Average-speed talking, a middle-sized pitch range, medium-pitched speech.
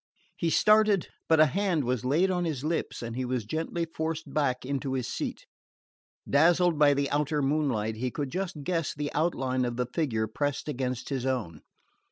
Yes: average, 185 wpm; average, 4.3 semitones; medium, 145 Hz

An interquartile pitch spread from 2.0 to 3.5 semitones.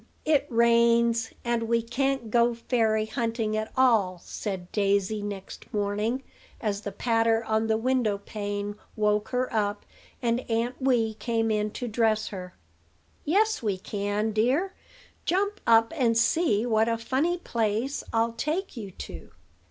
Yes: narrow, 2.4 semitones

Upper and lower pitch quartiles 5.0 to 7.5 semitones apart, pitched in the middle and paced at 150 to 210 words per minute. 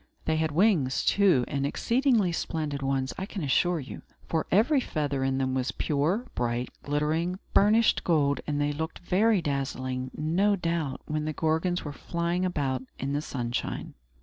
No: average, 4.5 semitones; medium, 155 Hz; average, 165 wpm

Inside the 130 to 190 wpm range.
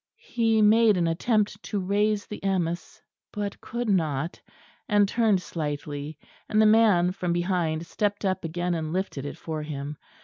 Yes: average, 160 wpm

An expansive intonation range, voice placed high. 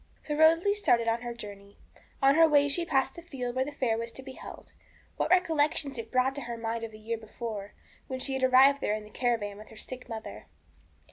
No: average, 3.9 semitones; very high, 255 Hz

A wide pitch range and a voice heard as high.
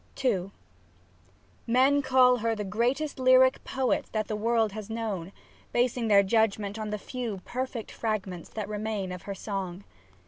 No: average, 3.7 semitones; high, 220 Hz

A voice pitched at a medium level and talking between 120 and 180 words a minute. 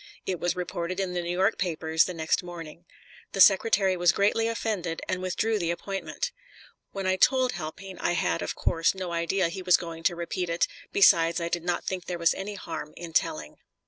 No: medium, 180 Hz; fast, 205 wpm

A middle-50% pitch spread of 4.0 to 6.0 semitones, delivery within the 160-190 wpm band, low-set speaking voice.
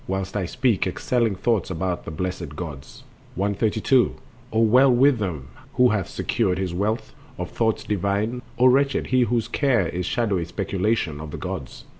Yes: average, 4.7 semitones; average, 165 wpm; low, 100 Hz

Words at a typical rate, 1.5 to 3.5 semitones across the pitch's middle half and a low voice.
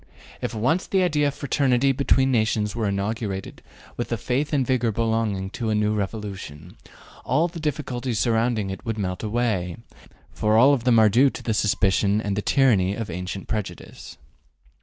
No: average, 170 wpm; average, 4.2 semitones; low, 110 Hz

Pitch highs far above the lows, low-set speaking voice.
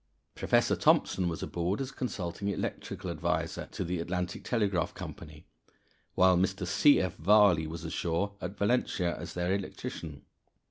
No: average, 2.9 semitones; very low, 90 Hz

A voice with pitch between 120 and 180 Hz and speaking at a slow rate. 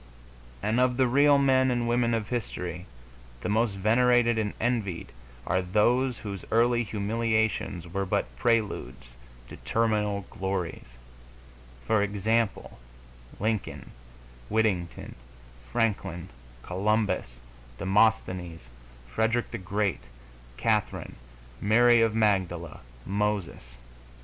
No: low, 105 Hz; slow, 100 wpm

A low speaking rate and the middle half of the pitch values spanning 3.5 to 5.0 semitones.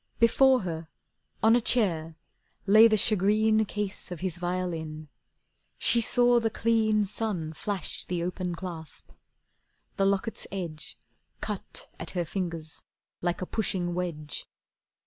Yes: slow, 125 wpm; average, 4.2 semitones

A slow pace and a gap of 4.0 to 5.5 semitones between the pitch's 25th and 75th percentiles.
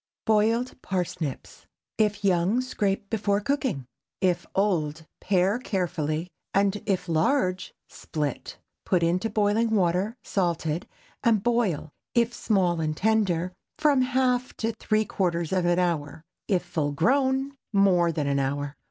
Yes: slow, 130 wpm; average, 4.7 semitones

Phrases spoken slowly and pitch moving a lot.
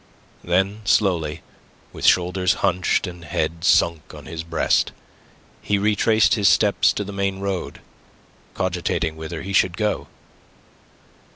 No: slow, 125 wpm; average, 2.8 semitones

